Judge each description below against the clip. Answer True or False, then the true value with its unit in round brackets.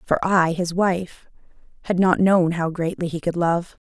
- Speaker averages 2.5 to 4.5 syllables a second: True (4.3 syllables/s)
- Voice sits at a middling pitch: True (175 Hz)